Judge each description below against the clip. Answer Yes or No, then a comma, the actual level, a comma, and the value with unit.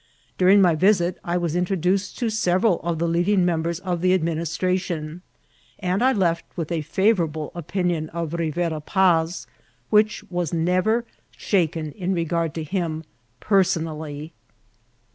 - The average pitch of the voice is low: No, medium, 175 Hz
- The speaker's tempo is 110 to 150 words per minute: Yes, average, 145 wpm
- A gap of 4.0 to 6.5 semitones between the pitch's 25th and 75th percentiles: No, narrow, 2.4 semitones